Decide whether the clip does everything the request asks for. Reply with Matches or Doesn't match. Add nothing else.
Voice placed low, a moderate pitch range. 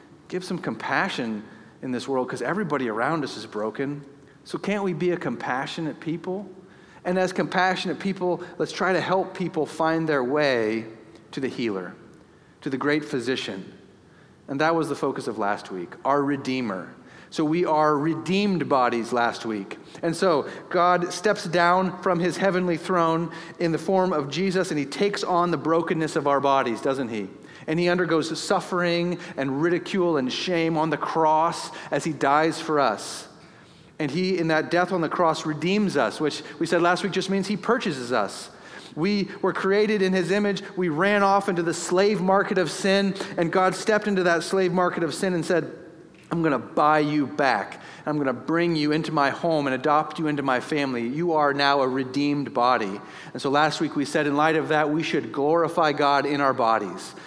Doesn't match